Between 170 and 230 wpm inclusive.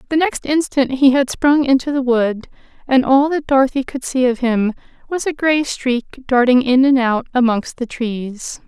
Yes: average, 195 wpm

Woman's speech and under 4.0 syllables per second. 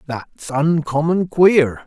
No: male; 2.9 syllables/s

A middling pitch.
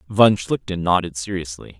No: very low, 90 Hz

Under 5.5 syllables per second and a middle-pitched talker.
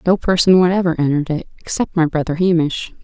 No: 6.2 syllables/s; medium, 170 Hz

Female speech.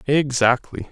No: male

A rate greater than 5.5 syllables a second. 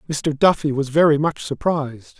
No: 5.1 syllables/s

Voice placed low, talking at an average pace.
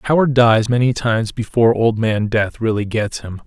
No: low, 115 Hz; fast, 210 wpm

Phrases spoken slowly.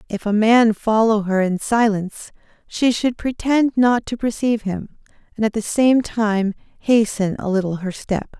No: average, 170 wpm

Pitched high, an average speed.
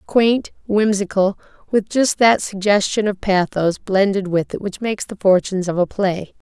Yes: high, 200 Hz; average, 165 wpm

